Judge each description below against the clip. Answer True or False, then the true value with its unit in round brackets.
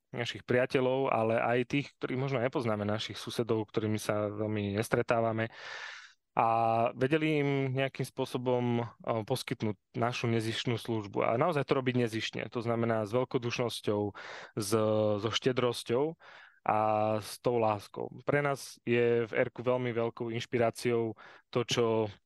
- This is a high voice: False (115 Hz)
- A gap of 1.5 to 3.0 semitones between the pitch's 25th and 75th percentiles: True (2.4 semitones)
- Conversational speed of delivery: True (130 wpm)